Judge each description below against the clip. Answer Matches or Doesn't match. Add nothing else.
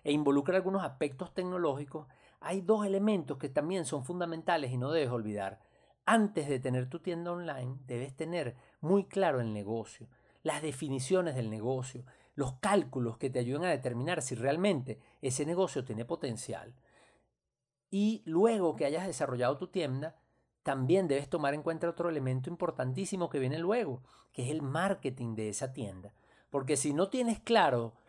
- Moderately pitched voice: Matches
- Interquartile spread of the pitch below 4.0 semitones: Doesn't match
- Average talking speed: Matches